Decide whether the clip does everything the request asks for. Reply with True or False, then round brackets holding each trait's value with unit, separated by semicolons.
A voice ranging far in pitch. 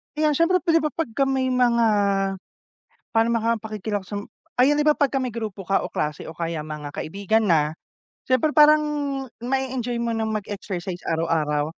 True (6.2 semitones)